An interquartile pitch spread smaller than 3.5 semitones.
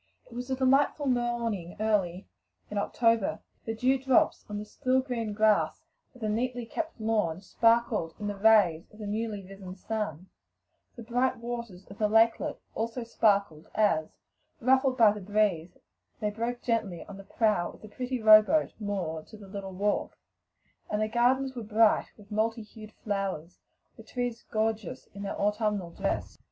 Yes: average, 2.7 semitones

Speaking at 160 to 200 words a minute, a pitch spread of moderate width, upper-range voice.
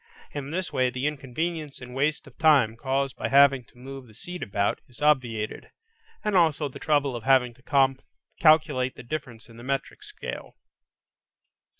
No: average, 170 wpm; average, 3.3 semitones; low, 135 Hz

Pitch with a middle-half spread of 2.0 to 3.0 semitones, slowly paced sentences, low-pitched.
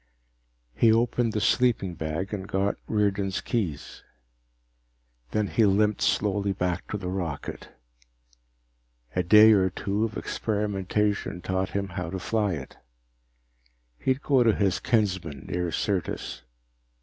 Yes: average, 2.7 semitones; slow, 125 wpm; low, 100 Hz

